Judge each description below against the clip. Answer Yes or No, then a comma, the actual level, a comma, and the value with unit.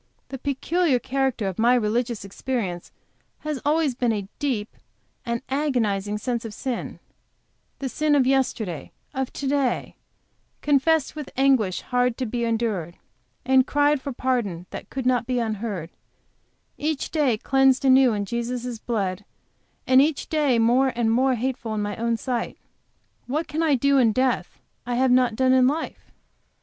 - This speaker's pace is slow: No, average, 160 wpm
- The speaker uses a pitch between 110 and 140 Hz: No, very high, 250 Hz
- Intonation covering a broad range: No, average, 3.0 semitones